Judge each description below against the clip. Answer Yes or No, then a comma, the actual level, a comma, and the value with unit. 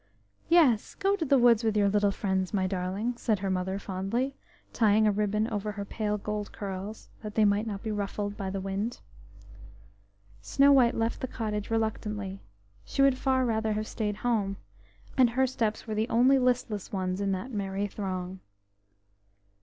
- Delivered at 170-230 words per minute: Yes, average, 175 wpm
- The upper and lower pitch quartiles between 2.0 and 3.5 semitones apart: Yes, average, 2.9 semitones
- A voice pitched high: Yes, high, 210 Hz